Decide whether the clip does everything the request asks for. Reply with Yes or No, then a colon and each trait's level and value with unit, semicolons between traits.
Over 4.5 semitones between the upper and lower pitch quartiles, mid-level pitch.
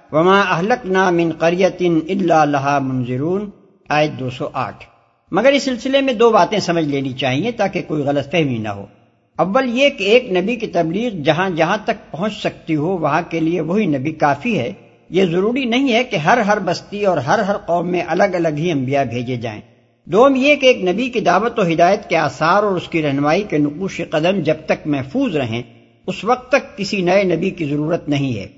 Yes: wide, 5.6 semitones; medium, 170 Hz